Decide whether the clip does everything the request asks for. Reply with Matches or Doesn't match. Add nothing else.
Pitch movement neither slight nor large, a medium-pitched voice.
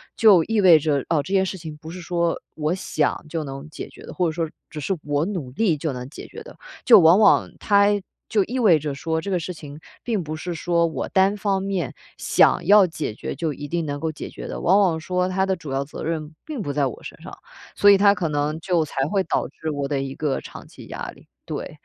Matches